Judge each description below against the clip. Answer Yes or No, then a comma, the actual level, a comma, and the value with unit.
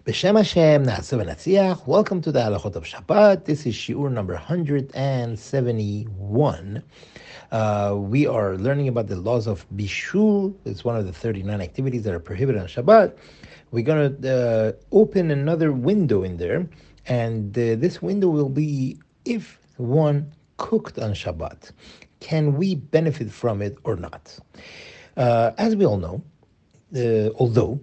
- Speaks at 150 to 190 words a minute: No, average, 140 wpm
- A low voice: Yes, low, 130 Hz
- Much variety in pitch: Yes, wide, 6.6 semitones